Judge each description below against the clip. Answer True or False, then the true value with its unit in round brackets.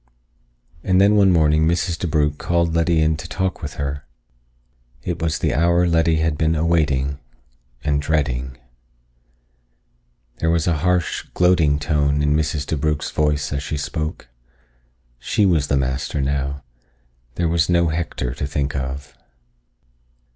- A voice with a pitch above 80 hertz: False (75 Hz)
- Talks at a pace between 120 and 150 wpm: True (140 wpm)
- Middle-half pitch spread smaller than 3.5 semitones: True (2.8 semitones)